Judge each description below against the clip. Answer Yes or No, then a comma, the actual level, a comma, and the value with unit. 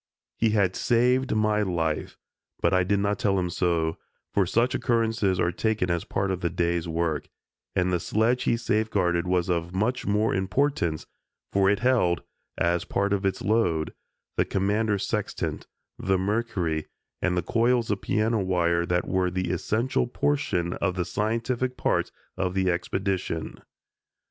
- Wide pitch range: No, average, 4.1 semitones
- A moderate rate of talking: Yes, average, 160 wpm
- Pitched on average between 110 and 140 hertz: No, very low, 95 Hz